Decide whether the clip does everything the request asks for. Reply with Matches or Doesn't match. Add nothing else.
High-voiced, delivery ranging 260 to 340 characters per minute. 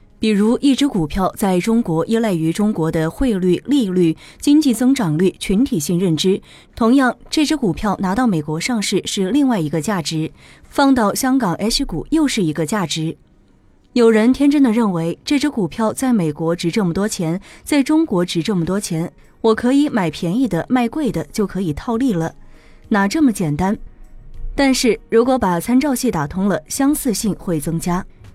Matches